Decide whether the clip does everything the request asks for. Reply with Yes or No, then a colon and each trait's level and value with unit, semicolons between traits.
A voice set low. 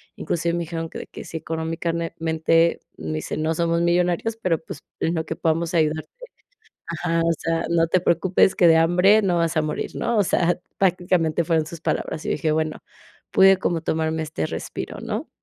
No: medium, 165 Hz